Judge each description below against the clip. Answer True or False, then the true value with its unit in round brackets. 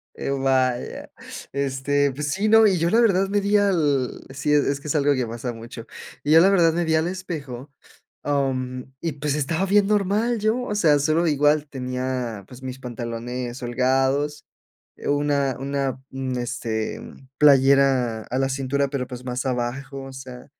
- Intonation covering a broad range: False (3.6 semitones)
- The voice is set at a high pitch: False (140 Hz)